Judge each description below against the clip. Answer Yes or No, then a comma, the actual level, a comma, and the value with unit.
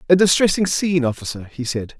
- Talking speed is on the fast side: No, average, 180 wpm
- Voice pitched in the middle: Yes, medium, 150 Hz